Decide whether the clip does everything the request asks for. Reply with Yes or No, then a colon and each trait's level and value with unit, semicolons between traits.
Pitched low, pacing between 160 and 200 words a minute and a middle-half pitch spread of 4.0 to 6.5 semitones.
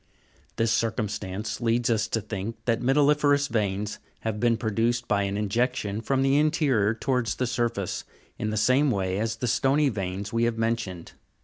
No: low, 115 Hz; average, 170 wpm; average, 3.2 semitones